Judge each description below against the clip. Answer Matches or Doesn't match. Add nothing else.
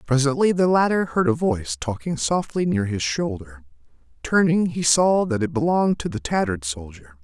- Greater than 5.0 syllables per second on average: Matches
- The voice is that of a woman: Doesn't match